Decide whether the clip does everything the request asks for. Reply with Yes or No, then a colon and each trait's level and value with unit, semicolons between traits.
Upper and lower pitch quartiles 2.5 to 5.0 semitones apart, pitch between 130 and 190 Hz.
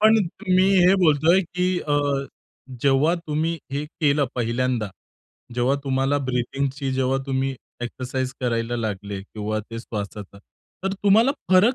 No: wide, 5.5 semitones; low, 135 Hz